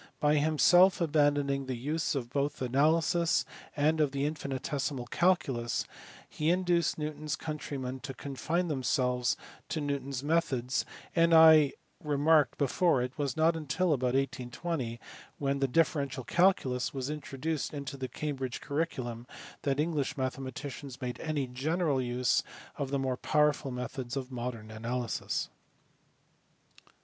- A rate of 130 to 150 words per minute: Yes, average, 140 wpm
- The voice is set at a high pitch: No, medium, 140 Hz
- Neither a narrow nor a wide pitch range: Yes, average, 3.2 semitones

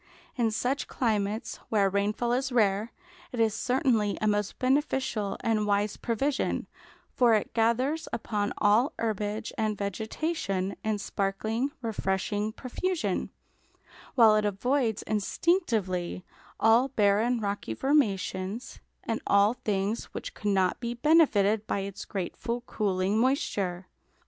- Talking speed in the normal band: No, slow, 125 wpm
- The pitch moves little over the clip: No, average, 3.4 semitones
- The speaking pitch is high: Yes, high, 215 Hz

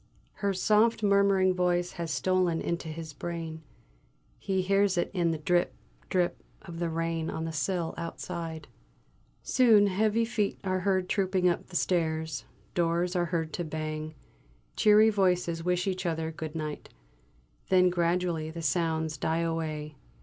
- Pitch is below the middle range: No, medium, 175 Hz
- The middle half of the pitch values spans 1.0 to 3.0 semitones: Yes, narrow, 2.5 semitones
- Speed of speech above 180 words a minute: No, average, 150 wpm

